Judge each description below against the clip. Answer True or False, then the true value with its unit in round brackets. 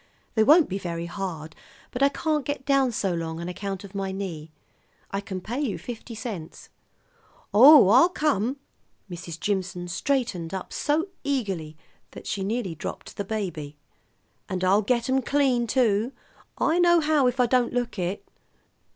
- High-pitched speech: True (210 Hz)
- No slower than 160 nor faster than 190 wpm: True (165 wpm)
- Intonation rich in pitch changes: True (6.3 semitones)